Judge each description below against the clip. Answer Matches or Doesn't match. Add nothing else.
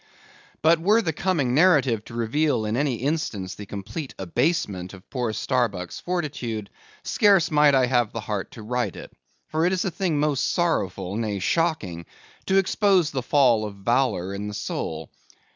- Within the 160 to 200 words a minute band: Matches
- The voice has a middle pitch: Doesn't match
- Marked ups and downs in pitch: Matches